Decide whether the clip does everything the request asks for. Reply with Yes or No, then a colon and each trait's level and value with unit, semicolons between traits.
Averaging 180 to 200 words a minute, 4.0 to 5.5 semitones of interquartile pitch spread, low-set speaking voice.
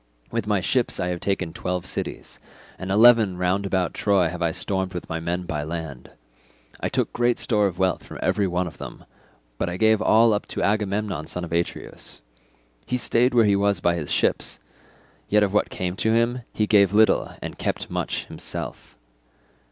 No: average, 190 wpm; average, 3.3 semitones; very low, 95 Hz